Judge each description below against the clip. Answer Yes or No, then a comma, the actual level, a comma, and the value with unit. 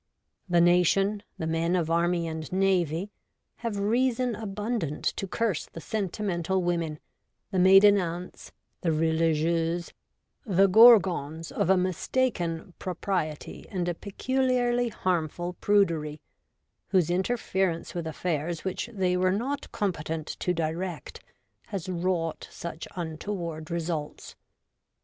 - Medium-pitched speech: Yes, medium, 180 Hz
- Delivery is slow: Yes, slow, 115 wpm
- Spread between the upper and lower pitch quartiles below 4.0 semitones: Yes, average, 3.3 semitones